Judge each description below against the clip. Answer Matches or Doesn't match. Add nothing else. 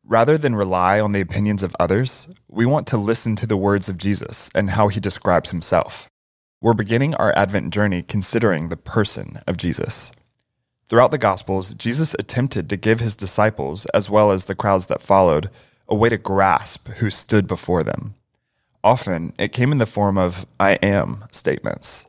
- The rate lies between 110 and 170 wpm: Doesn't match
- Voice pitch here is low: Matches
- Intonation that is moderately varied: Matches